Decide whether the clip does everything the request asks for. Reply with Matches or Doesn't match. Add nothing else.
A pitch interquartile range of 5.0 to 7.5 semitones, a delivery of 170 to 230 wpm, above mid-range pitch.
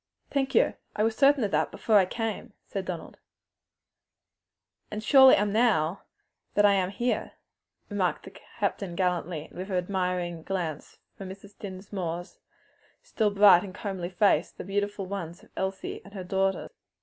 Doesn't match